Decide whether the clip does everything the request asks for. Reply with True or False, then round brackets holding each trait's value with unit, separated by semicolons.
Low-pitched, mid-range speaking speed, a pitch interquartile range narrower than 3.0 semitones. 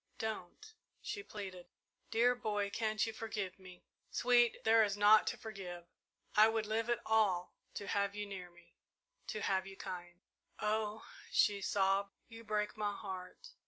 False (210 Hz; 160 wpm; 2.5 semitones)